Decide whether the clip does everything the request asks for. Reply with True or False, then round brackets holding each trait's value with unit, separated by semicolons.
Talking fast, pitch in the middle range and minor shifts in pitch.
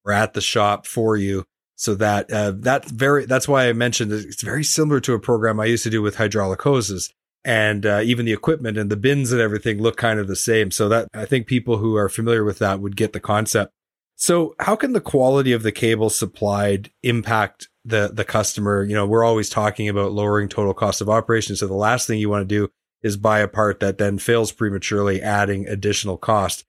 False (225 wpm; 110 Hz; 2.2 semitones)